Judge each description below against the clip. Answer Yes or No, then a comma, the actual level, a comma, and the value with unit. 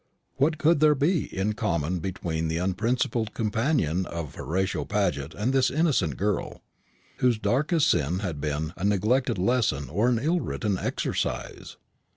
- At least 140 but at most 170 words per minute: Yes, average, 150 wpm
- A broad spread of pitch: Yes, wide, 7.1 semitones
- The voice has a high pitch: No, low, 105 Hz